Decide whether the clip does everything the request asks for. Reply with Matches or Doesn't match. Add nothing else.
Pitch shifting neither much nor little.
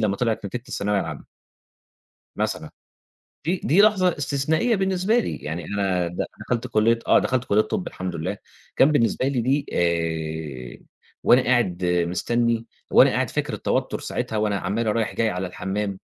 Doesn't match